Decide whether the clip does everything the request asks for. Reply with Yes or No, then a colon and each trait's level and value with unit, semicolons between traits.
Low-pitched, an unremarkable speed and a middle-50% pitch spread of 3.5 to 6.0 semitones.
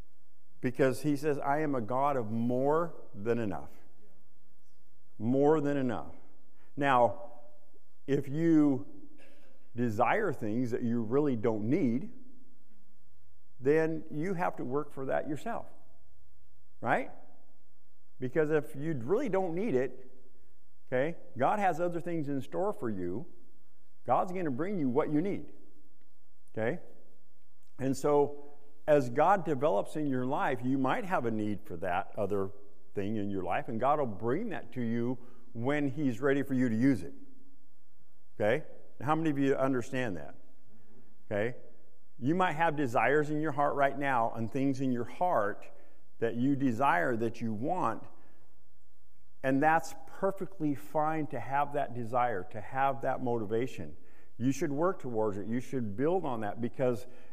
Yes: low, 130 Hz; average, 150 wpm; average, 4.7 semitones